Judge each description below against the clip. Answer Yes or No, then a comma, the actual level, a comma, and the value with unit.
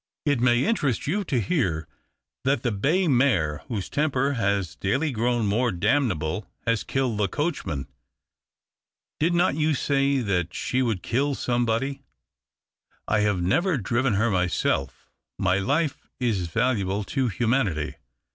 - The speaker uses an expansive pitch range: Yes, wide, 5.9 semitones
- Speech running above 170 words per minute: No, average, 140 wpm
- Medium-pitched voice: No, low, 120 Hz